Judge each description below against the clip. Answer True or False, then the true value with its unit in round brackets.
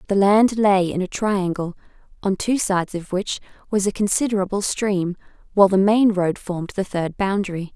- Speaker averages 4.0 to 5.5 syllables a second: True (5.1 syllables/s)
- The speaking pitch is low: False (195 Hz)